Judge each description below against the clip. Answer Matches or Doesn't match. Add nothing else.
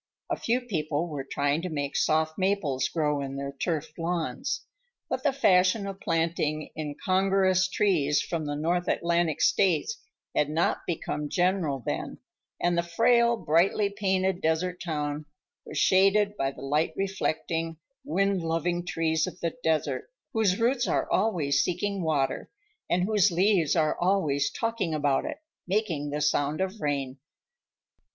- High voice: Doesn't match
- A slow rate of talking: Doesn't match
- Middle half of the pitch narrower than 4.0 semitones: Doesn't match